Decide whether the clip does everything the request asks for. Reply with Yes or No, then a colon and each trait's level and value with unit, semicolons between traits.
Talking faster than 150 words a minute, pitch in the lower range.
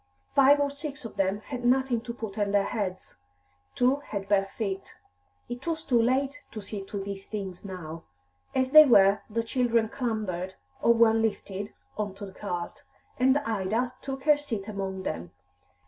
No: average, 175 wpm; high, 220 Hz